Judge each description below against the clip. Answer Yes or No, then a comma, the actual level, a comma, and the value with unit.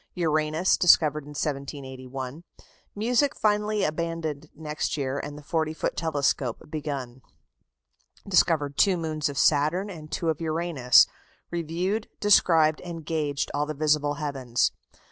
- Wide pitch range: No, average, 2.7 semitones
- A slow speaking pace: Yes, slow, 125 wpm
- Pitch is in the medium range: Yes, medium, 155 Hz